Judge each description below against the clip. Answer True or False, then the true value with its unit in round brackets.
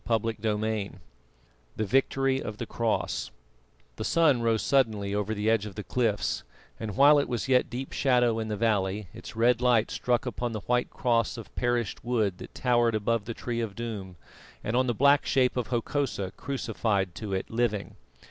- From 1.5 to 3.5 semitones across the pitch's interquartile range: True (2.7 semitones)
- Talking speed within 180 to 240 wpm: True (185 wpm)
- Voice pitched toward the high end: False (115 Hz)